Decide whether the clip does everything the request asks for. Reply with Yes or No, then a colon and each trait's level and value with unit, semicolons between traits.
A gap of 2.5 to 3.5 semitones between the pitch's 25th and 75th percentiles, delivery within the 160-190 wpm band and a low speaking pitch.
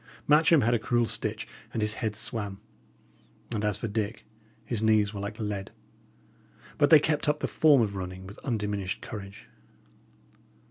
Yes: average, 2.8 semitones; average, 165 wpm; low, 110 Hz